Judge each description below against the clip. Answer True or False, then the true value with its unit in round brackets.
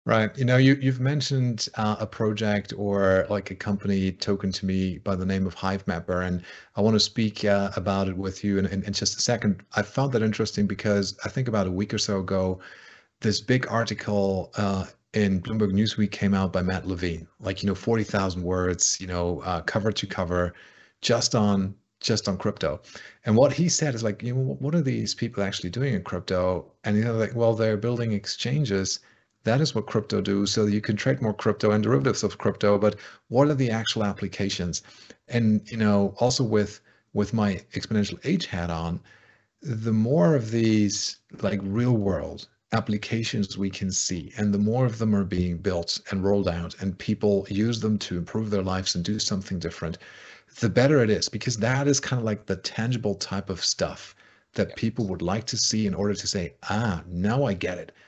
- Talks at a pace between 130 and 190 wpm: False (205 wpm)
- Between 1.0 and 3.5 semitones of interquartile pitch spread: True (2.7 semitones)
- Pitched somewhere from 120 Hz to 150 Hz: False (105 Hz)